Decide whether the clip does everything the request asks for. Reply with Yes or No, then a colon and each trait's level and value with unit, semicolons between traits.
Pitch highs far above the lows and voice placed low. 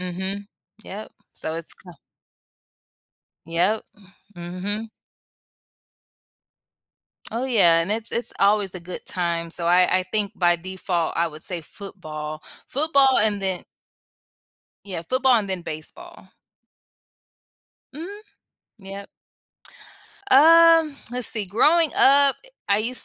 No: wide, 6.0 semitones; high, 195 Hz